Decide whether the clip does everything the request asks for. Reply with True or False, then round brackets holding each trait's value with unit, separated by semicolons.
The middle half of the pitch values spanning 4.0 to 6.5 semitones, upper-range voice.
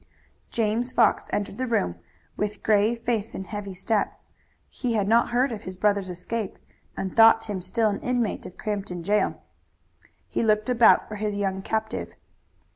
False (2.4 semitones; 210 Hz)